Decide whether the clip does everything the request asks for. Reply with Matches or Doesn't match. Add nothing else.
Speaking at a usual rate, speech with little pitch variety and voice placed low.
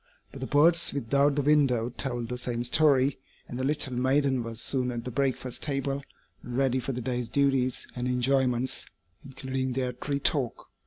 Matches